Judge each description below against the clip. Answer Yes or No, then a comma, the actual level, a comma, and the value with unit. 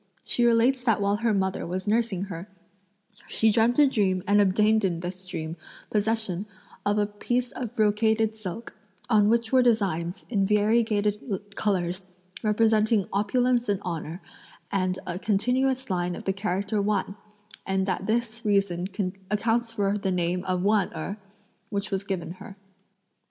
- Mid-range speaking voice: No, high, 205 Hz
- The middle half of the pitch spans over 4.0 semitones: No, average, 2.8 semitones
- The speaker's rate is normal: Yes, average, 150 wpm